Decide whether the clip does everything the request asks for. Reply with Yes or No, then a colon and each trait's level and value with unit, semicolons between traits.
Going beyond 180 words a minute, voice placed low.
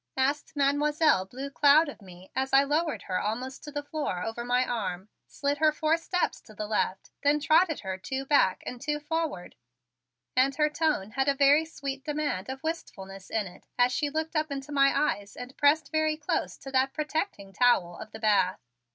No: average, 195 wpm; very high, 275 Hz